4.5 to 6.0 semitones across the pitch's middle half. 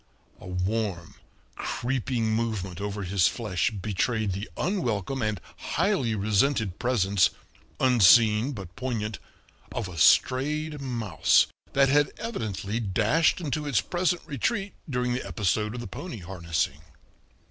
Yes: average, 5.2 semitones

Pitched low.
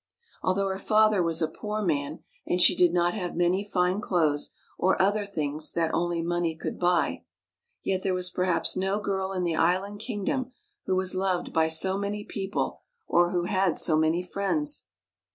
No: medium, 185 Hz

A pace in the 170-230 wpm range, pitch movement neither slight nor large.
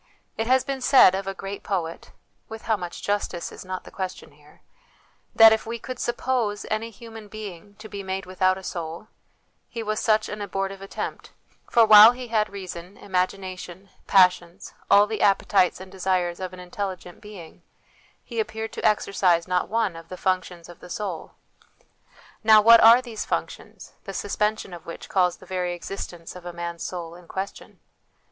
Yes: average, 180 wpm; average, 3.1 semitones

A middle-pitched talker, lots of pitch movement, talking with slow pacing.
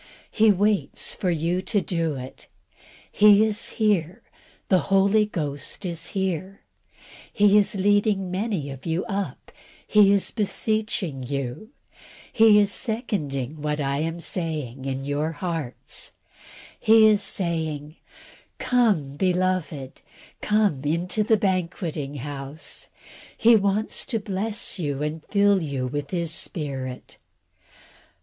Yes: medium, 180 Hz; wide, 5.7 semitones; slow, 115 wpm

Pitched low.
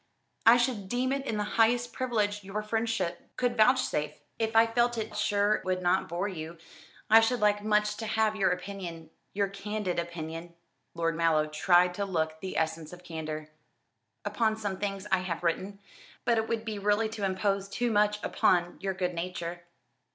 No: high, 200 Hz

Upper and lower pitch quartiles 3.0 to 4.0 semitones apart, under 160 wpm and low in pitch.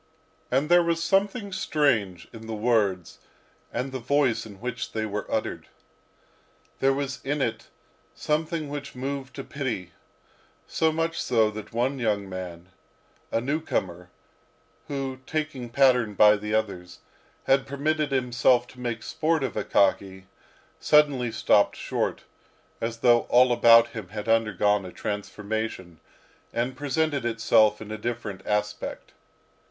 No: average, 4.7 semitones; slow, 135 wpm; low, 120 Hz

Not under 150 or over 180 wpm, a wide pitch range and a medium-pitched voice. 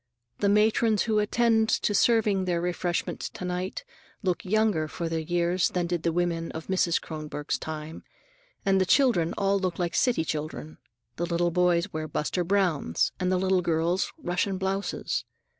No: average, 165 wpm; average, 2.8 semitones; medium, 180 Hz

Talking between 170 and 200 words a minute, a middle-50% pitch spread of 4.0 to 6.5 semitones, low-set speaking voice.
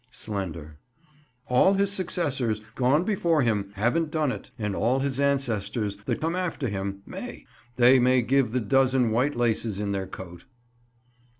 No: average, 145 wpm; average, 5.2 semitones; low, 125 Hz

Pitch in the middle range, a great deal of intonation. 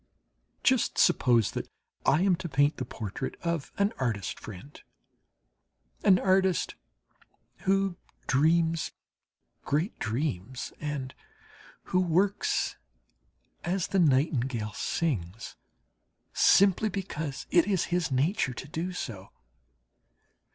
Yes: medium, 155 Hz; wide, 6.0 semitones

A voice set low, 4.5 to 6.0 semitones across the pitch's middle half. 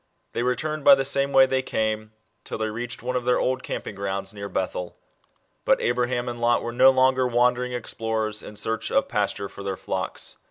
No: low, 120 Hz; average, 3.1 semitones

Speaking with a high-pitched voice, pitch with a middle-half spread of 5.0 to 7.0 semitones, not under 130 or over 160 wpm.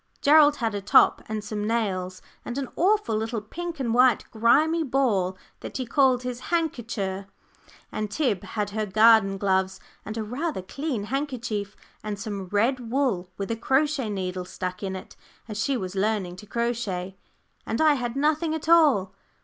No: high, 225 Hz; average, 5.3 semitones; average, 170 wpm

